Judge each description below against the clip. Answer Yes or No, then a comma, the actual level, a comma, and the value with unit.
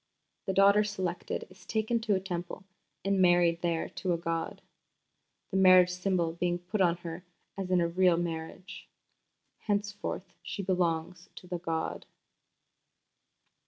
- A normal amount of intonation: No, narrow, 2.1 semitones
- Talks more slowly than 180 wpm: Yes, average, 140 wpm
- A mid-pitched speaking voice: Yes, medium, 180 Hz